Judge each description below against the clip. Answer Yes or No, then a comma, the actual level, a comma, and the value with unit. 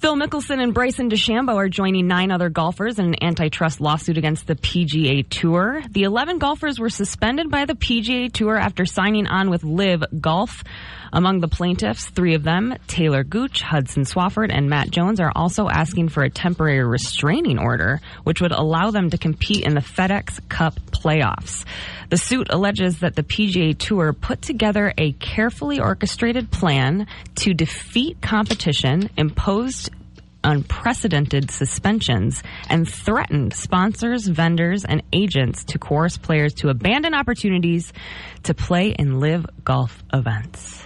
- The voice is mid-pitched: Yes, medium, 175 Hz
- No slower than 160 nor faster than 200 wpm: No, average, 150 wpm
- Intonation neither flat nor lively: No, wide, 5.8 semitones